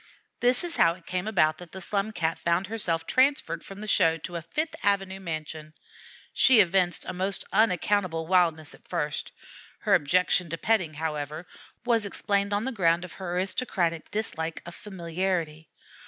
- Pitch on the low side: No, medium, 180 Hz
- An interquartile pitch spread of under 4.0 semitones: Yes, average, 3.6 semitones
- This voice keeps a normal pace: Yes, average, 170 wpm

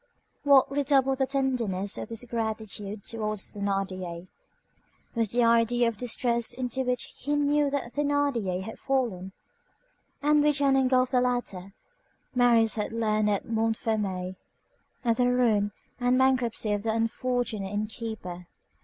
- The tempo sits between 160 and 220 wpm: No, average, 140 wpm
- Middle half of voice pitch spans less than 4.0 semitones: Yes, average, 3.6 semitones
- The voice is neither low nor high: No, high, 230 Hz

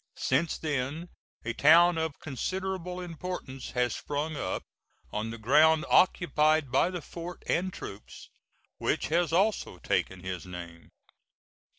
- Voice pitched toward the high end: No, medium, 155 Hz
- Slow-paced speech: Yes, slow, 125 wpm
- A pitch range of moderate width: No, wide, 5.8 semitones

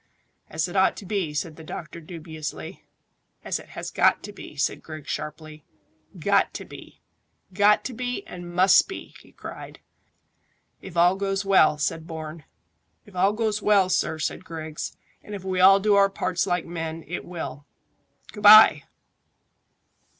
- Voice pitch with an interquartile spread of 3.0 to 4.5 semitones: Yes, average, 3.8 semitones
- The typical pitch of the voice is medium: Yes, medium, 175 Hz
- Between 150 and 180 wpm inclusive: Yes, average, 165 wpm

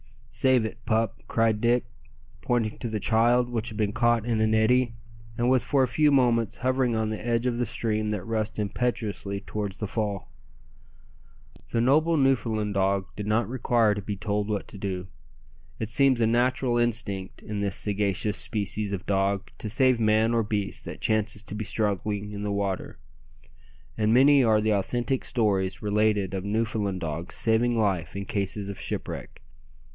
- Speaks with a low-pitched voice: Yes, low, 110 Hz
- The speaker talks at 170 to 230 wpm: Yes, average, 175 wpm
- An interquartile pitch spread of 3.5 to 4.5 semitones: No, narrow, 2.6 semitones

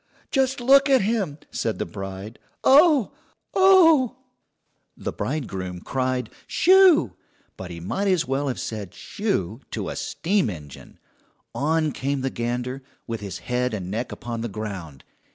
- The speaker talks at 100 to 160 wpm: Yes, average, 145 wpm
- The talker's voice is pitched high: No, low, 130 Hz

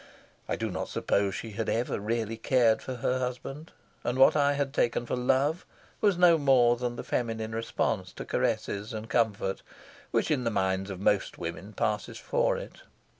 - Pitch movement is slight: No, average, 3.5 semitones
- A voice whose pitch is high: No, low, 120 Hz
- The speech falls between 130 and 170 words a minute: No, average, 180 wpm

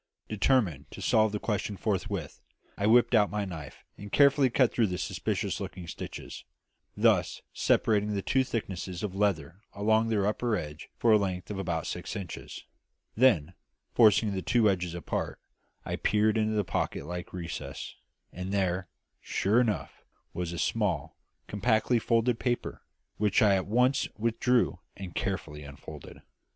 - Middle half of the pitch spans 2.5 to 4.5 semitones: Yes, average, 3.6 semitones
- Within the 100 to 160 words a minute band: Yes, average, 155 wpm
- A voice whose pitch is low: Yes, low, 100 Hz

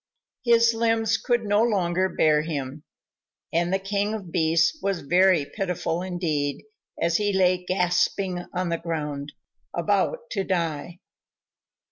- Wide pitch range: No, average, 3.5 semitones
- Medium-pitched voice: Yes, medium, 180 Hz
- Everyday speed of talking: No, slow, 130 wpm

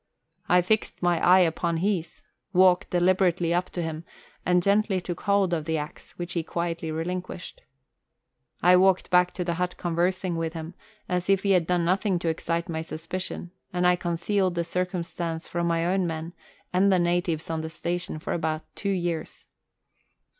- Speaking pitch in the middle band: Yes, medium, 175 Hz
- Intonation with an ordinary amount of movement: No, narrow, 1.6 semitones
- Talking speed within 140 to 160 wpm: No, average, 180 wpm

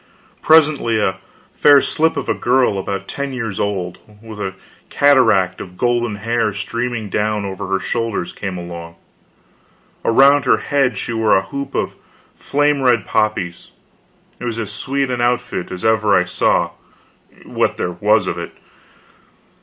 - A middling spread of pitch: Yes, average, 4.4 semitones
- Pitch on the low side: Yes, low, 110 Hz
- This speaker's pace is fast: No, average, 155 wpm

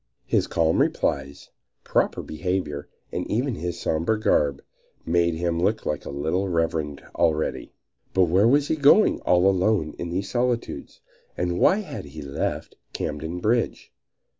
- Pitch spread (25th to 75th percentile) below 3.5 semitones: No, wide, 5.4 semitones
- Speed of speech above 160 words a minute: No, average, 145 wpm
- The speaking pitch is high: No, very low, 85 Hz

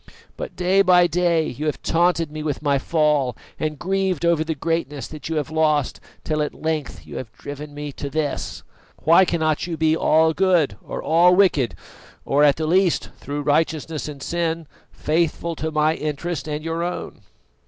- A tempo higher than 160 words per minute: Yes, average, 180 wpm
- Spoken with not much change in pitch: Yes, narrow, 2.3 semitones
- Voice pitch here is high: No, medium, 155 Hz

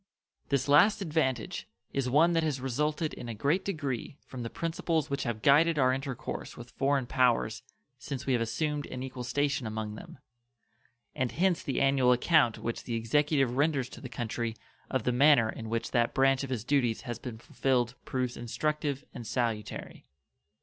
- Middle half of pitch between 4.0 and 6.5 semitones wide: No, average, 3.6 semitones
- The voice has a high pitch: No, low, 130 Hz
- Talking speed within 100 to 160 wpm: No, average, 175 wpm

